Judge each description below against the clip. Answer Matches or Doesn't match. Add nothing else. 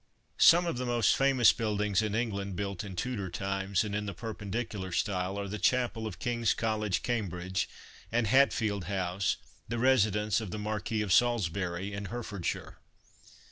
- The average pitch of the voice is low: Matches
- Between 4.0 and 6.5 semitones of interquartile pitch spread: Doesn't match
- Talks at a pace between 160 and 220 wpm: Matches